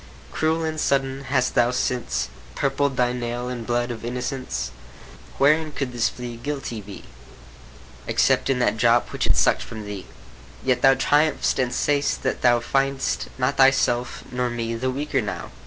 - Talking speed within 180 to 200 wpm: No, average, 165 wpm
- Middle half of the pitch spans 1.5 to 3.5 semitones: Yes, narrow, 2.4 semitones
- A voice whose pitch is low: Yes, low, 125 Hz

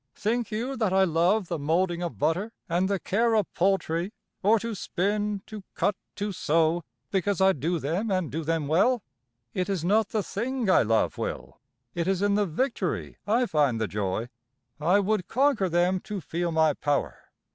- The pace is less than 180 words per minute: No, average, 185 wpm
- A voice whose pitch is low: No, medium, 185 Hz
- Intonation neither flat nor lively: Yes, average, 4.2 semitones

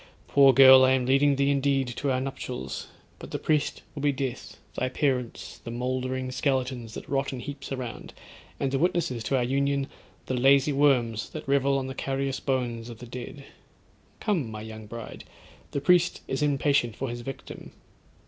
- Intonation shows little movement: Yes, narrow, 2.1 semitones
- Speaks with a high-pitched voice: No, low, 135 Hz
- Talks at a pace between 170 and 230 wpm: Yes, average, 180 wpm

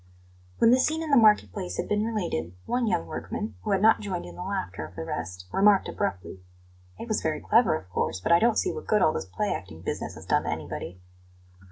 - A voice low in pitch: No, medium, 185 Hz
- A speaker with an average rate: No, fast, 235 wpm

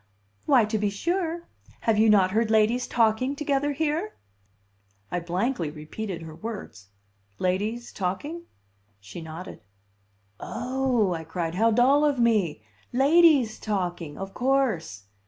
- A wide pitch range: Yes, wide, 6.8 semitones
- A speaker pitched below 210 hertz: No, high, 220 Hz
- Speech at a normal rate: No, slow, 125 wpm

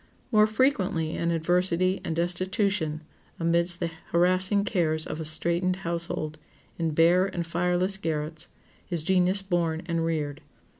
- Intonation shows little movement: Yes, narrow, 2.1 semitones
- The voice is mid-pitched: Yes, medium, 170 Hz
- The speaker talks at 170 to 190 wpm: No, slow, 135 wpm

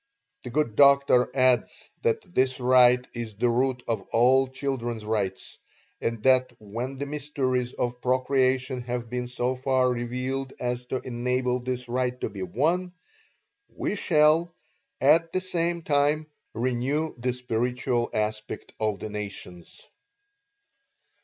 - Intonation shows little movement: Yes, narrow, 2.1 semitones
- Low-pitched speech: Yes, low, 125 Hz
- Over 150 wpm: No, slow, 135 wpm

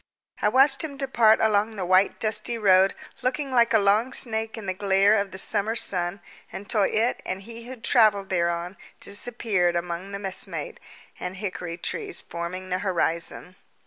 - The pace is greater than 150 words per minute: Yes, average, 165 wpm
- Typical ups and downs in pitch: Yes, average, 3.7 semitones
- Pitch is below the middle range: No, high, 205 Hz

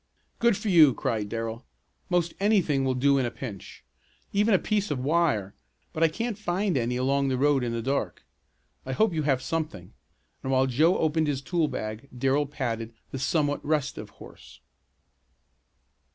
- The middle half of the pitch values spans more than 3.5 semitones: Yes, average, 4.7 semitones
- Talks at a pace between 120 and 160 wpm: No, average, 170 wpm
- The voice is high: No, medium, 140 Hz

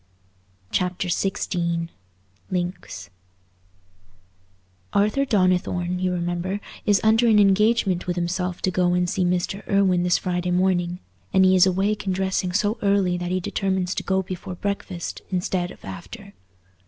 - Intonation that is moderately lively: No, narrow, 1.8 semitones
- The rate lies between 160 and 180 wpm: No, average, 140 wpm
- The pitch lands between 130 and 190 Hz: Yes, medium, 185 Hz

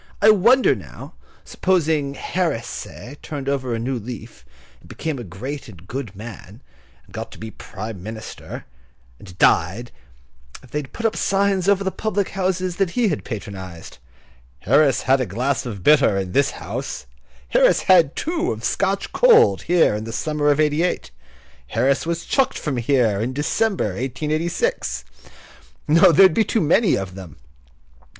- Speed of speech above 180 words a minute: No, average, 165 wpm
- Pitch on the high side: No, medium, 140 Hz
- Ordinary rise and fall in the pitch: No, wide, 8.1 semitones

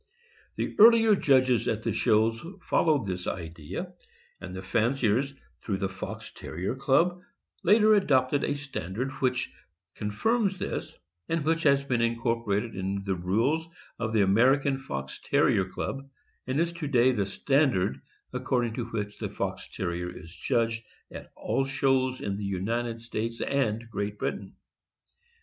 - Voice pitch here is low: Yes, low, 115 Hz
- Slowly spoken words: No, average, 150 wpm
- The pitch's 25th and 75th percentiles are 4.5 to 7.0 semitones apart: Yes, wide, 5.4 semitones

